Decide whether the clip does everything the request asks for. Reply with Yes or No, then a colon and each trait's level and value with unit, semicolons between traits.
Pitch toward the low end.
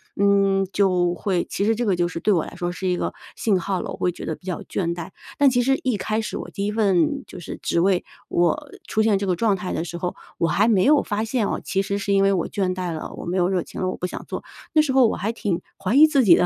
No: high, 195 Hz